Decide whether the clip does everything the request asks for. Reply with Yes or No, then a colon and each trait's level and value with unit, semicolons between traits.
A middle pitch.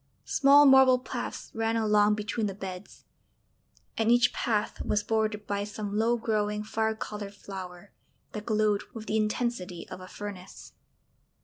No: high, 210 Hz